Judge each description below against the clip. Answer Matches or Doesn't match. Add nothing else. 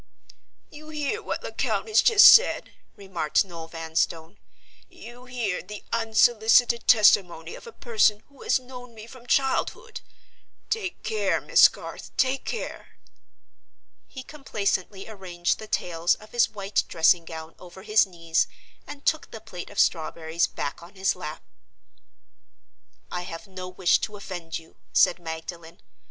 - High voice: Matches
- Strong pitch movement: Matches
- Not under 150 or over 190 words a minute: Doesn't match